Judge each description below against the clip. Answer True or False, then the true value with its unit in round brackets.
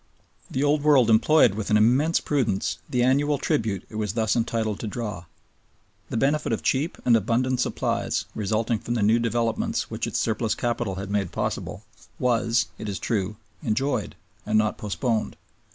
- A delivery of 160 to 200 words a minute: True (170 wpm)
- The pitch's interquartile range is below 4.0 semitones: True (3.0 semitones)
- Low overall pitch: True (115 Hz)